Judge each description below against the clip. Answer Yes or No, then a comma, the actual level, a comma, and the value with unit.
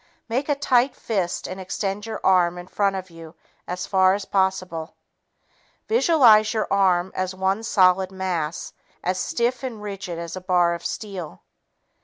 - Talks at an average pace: Yes, average, 160 wpm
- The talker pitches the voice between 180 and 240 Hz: Yes, high, 190 Hz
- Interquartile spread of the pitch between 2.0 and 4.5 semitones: Yes, average, 3.0 semitones